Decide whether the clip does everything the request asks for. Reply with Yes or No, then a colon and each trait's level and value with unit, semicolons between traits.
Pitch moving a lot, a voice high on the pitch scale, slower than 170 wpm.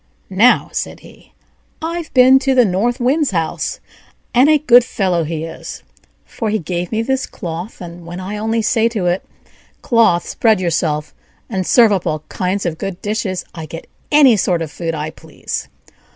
No: wide, 5.8 semitones; high, 195 Hz; average, 180 wpm